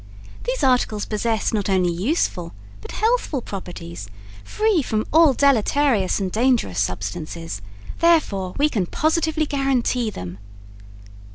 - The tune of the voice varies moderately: No, wide, 8.3 semitones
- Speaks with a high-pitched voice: Yes, high, 225 Hz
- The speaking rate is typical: No, slow, 115 wpm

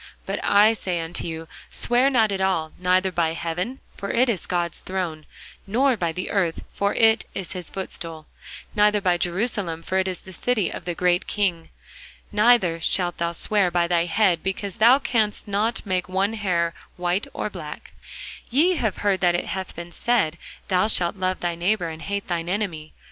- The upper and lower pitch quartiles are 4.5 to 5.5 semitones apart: No, average, 3.4 semitones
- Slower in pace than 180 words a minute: No, average, 185 wpm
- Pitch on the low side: No, medium, 185 Hz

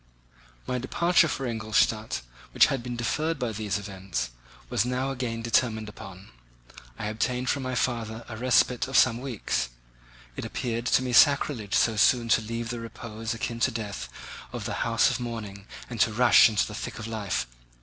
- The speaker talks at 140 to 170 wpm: No, average, 180 wpm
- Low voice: Yes, low, 115 Hz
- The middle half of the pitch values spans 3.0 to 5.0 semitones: No, narrow, 2.5 semitones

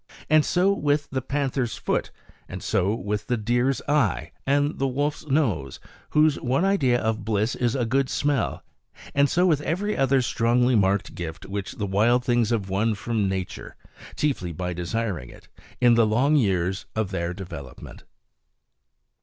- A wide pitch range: Yes, wide, 5.8 semitones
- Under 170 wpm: Yes, average, 160 wpm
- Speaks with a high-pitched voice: No, low, 120 Hz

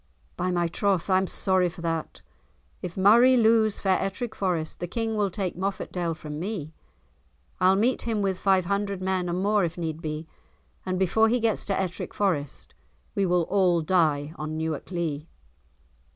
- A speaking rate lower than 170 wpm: No, average, 175 wpm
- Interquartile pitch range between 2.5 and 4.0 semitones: Yes, average, 3.2 semitones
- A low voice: No, medium, 185 Hz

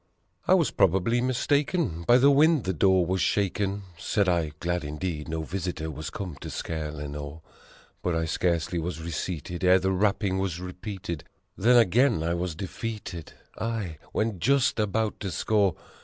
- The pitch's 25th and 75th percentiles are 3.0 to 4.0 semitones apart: No, average, 4.6 semitones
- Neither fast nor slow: Yes, average, 160 wpm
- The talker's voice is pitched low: Yes, very low, 95 Hz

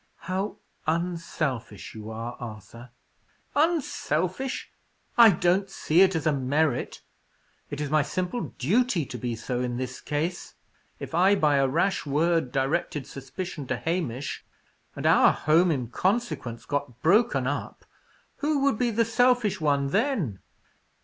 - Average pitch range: No, wide, 6.6 semitones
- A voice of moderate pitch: Yes, medium, 155 Hz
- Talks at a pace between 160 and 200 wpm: No, average, 140 wpm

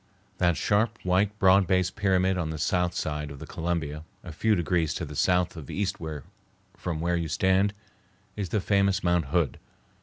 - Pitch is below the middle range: Yes, very low, 90 Hz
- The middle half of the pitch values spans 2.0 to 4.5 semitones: Yes, average, 3.1 semitones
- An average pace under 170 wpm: No, average, 180 wpm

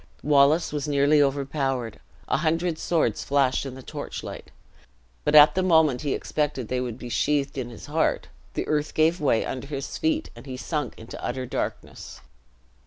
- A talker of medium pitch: Yes, medium, 145 Hz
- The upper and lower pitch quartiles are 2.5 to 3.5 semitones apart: Yes, average, 2.8 semitones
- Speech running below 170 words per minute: No, average, 175 wpm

